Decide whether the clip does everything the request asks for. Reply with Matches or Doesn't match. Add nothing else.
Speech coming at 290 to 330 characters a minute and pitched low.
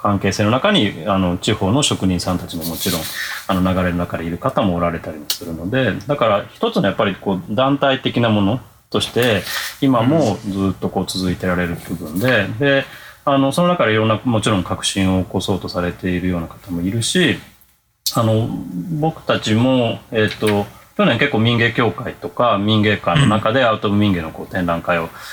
Doesn't match